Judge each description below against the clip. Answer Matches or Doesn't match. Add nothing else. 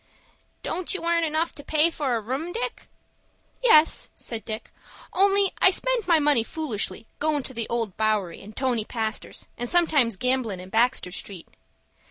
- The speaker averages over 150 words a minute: Matches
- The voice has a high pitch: Matches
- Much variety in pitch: Matches